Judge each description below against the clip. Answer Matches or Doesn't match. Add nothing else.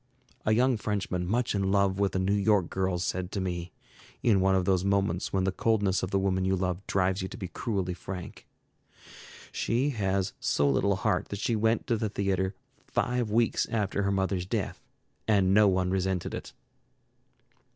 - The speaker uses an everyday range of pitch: Doesn't match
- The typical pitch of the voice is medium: Doesn't match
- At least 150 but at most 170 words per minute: Doesn't match